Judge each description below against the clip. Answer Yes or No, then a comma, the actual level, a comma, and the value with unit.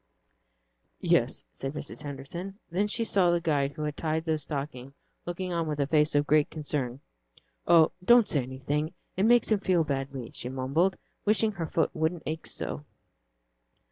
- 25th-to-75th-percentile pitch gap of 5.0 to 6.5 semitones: No, average, 4.0 semitones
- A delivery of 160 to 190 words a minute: Yes, average, 170 wpm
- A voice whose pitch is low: No, medium, 155 Hz